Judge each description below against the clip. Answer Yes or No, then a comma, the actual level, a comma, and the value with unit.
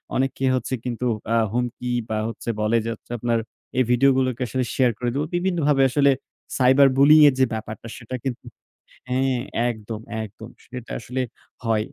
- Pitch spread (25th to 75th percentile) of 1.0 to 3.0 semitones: Yes, narrow, 2.5 semitones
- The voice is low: Yes, low, 125 Hz